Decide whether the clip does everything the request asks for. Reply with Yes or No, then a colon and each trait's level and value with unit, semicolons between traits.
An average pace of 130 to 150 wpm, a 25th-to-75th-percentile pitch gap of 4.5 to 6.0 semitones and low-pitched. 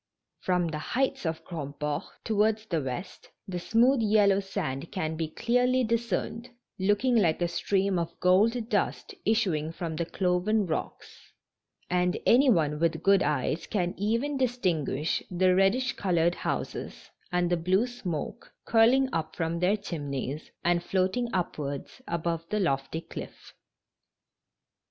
No: slow, 135 wpm; average, 5.0 semitones; medium, 180 Hz